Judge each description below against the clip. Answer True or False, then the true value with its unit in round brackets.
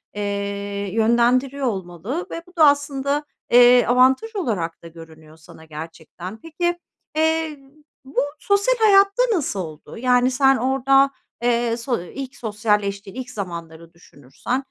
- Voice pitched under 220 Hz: False (245 Hz)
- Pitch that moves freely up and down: True (6.3 semitones)